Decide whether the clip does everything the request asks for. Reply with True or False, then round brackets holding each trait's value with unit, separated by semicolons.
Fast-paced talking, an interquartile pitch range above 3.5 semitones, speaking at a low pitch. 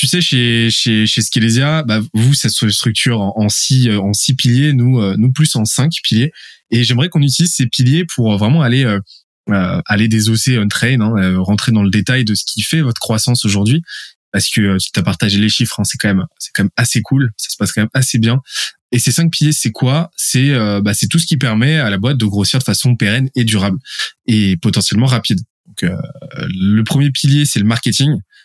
True (225 wpm; 4.0 semitones; 115 Hz)